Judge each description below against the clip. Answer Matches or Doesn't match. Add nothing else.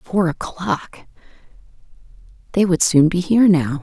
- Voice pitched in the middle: Matches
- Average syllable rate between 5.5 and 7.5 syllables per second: Doesn't match